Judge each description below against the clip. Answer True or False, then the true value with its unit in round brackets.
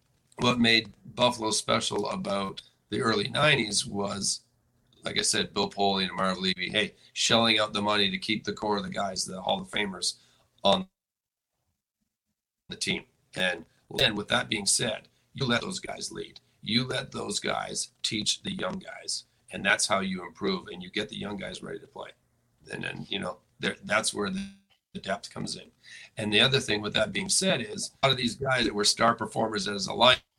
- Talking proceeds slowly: False (195 wpm)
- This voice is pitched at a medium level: False (110 Hz)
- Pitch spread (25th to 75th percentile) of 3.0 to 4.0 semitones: True (3.6 semitones)